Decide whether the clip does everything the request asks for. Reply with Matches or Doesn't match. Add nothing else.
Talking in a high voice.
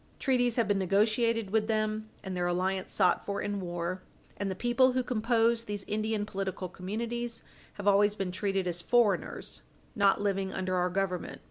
Matches